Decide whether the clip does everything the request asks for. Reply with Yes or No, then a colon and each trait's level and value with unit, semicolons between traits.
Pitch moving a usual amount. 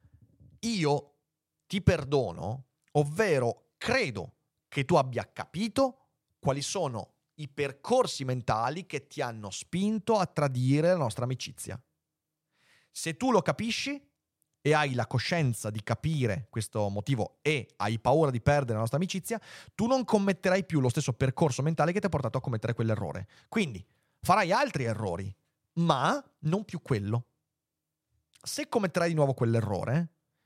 No: wide, 6.3 semitones